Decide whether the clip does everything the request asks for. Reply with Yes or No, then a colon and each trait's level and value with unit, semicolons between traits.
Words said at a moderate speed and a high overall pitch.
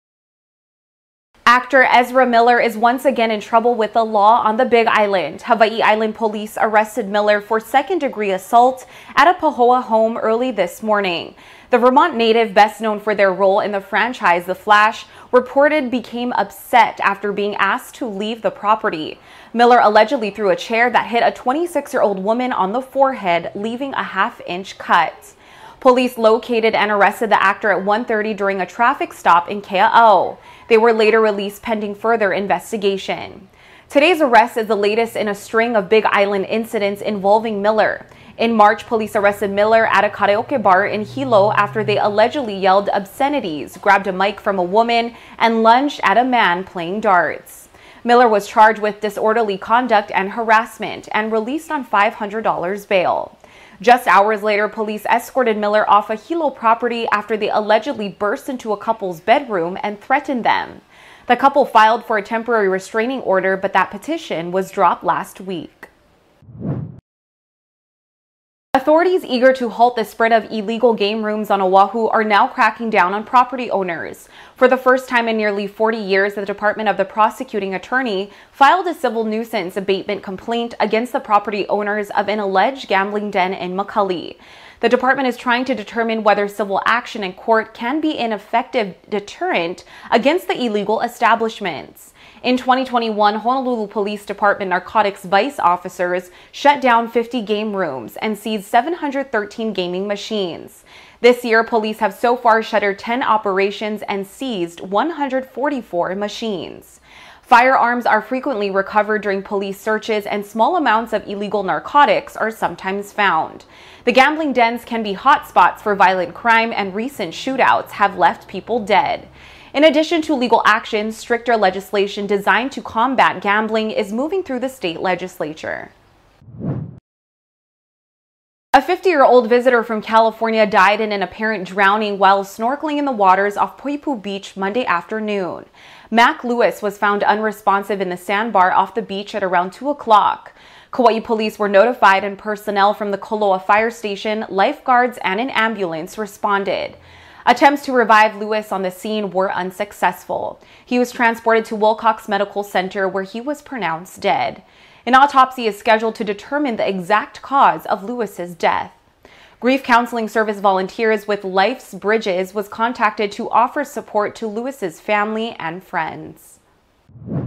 Yes: average, 155 wpm; high, 215 Hz